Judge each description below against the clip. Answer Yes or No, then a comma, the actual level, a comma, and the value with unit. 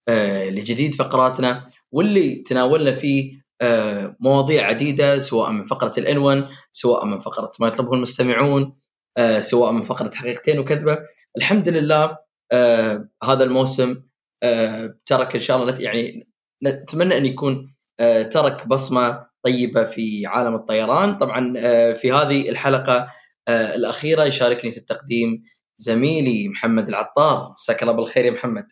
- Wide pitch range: No, average, 3.0 semitones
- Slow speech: No, fast, 135 wpm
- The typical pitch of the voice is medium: No, low, 130 Hz